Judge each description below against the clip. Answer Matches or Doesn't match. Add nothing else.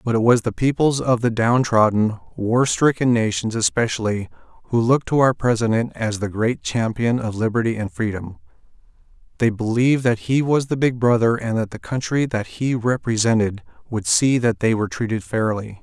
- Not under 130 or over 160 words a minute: Doesn't match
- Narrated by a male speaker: Matches